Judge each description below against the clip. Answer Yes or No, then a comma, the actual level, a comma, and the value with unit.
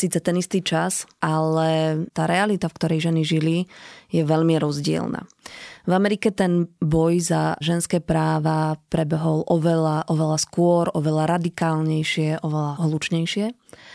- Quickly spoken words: No, average, 125 wpm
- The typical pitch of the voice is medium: Yes, medium, 165 Hz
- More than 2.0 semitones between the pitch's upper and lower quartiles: No, narrow, 1.6 semitones